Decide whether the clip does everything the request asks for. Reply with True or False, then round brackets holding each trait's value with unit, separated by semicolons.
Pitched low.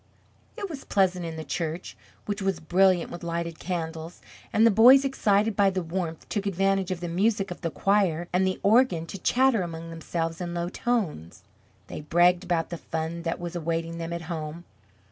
False (175 Hz)